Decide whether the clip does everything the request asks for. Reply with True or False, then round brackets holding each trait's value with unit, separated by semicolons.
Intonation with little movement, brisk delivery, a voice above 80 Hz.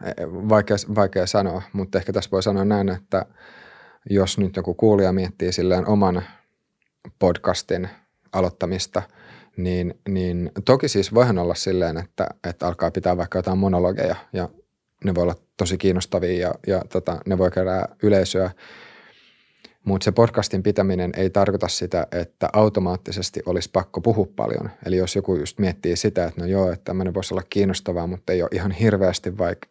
True (1.7 semitones; 160 wpm; 95 Hz)